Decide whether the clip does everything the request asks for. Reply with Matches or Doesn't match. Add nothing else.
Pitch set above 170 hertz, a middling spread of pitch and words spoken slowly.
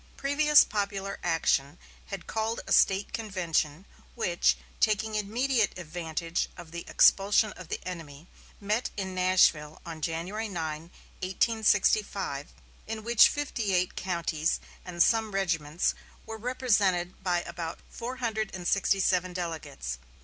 Matches